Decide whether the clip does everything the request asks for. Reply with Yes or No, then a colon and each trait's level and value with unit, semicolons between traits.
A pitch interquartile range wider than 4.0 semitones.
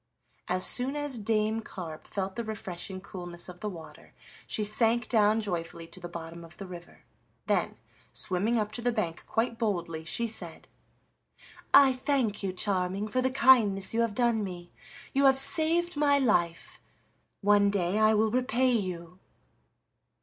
Yes: average, 4.7 semitones